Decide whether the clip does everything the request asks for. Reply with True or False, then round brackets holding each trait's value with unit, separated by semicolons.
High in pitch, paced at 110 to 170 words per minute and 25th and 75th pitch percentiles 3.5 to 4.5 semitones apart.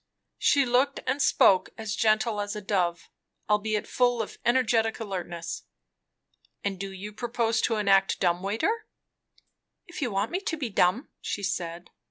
True (215 Hz; 155 wpm; 3.8 semitones)